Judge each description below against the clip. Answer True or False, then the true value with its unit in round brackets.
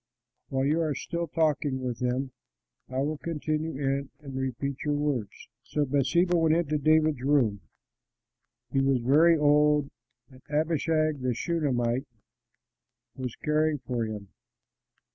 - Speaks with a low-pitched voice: False (145 Hz)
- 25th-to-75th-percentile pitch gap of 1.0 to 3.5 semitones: True (3.1 semitones)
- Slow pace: True (130 wpm)